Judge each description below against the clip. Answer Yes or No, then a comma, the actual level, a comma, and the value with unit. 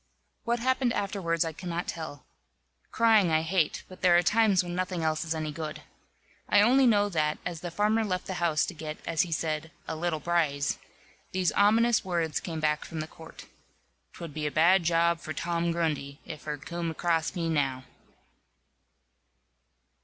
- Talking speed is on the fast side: No, average, 175 wpm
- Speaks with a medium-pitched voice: Yes, medium, 170 Hz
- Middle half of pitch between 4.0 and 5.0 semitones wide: No, average, 2.8 semitones